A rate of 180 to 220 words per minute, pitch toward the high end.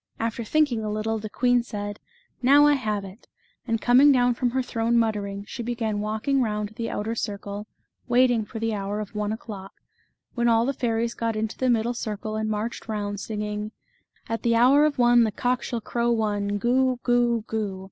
Yes: average, 200 wpm; high, 225 Hz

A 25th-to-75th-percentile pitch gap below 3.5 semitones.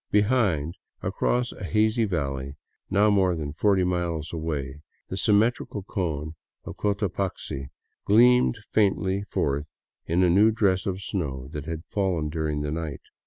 No: average, 5.1 semitones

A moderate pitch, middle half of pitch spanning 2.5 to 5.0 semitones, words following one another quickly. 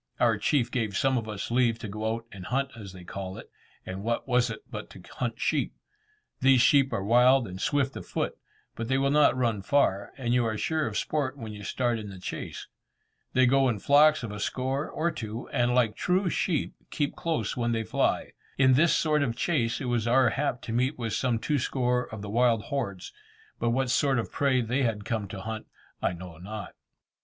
No: low, 120 Hz; average, 3.7 semitones; fast, 220 wpm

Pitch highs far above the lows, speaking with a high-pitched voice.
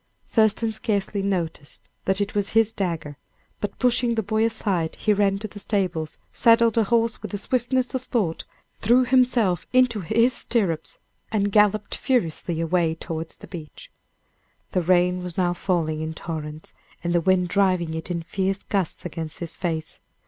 No: average, 4.7 semitones; high, 195 Hz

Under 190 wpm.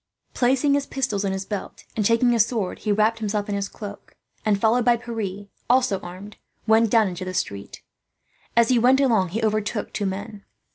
No: average, 195 wpm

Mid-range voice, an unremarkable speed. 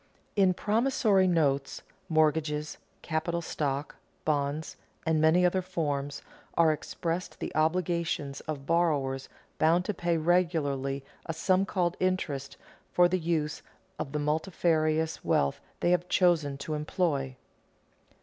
No: medium, 160 Hz; slow, 120 wpm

